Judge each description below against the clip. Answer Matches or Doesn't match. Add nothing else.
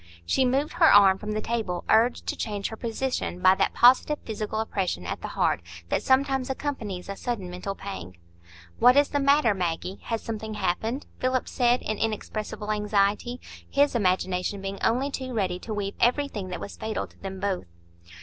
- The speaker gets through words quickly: Doesn't match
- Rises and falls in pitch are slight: Doesn't match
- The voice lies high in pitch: Matches